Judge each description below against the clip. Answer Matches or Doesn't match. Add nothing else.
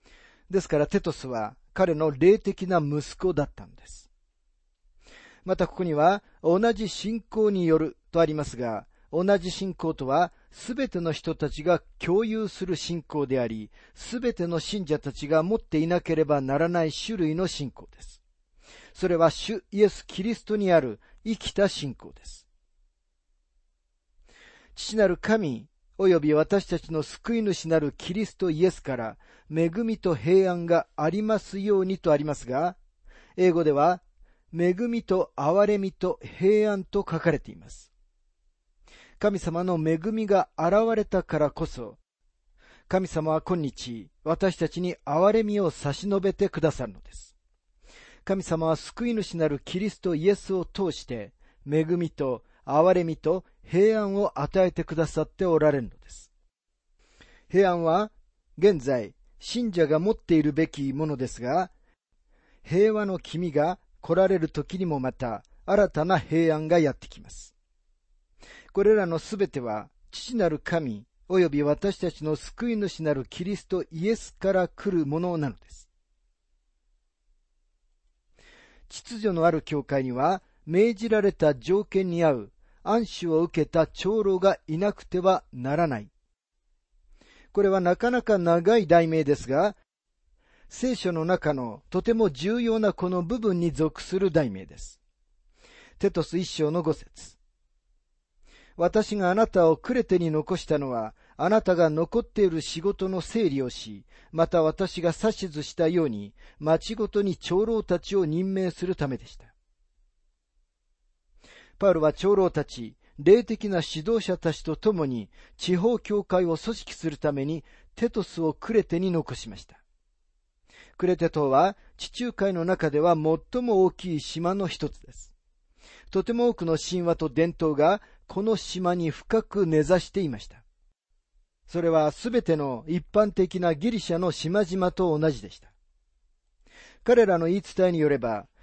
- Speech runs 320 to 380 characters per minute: Doesn't match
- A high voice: Doesn't match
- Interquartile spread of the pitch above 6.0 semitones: Doesn't match